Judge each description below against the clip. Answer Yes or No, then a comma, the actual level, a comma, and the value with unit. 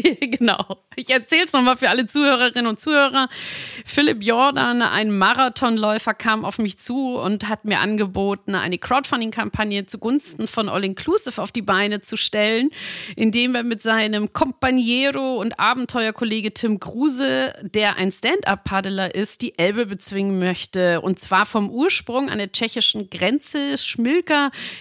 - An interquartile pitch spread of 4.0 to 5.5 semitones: Yes, average, 4.5 semitones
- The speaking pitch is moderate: No, high, 225 Hz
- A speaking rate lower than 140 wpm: No, average, 145 wpm